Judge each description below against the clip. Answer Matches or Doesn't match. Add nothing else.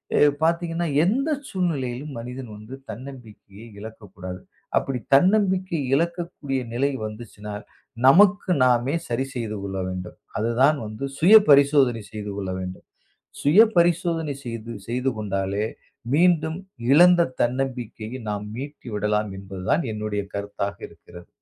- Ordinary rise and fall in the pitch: Doesn't match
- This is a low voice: Matches